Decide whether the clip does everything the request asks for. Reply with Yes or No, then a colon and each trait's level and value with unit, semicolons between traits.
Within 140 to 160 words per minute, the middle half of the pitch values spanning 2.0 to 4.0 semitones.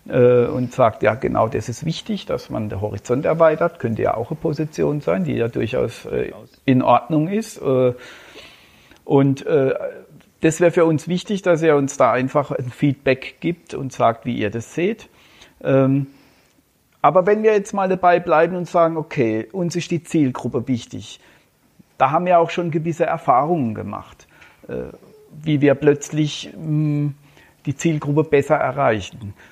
No: average, 150 wpm; average, 4.8 semitones